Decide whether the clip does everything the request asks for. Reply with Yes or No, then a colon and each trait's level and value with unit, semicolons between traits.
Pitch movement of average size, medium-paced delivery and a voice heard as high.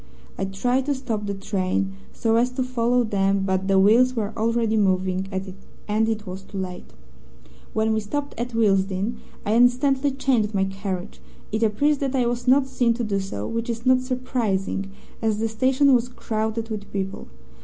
Yes: average, 4.1 semitones; average, 180 wpm; high, 220 Hz